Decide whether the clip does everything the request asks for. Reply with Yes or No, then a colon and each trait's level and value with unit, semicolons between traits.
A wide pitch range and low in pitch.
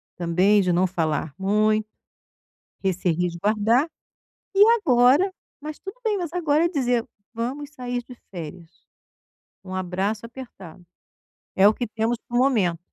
No: wide, 6.0 semitones; high, 220 Hz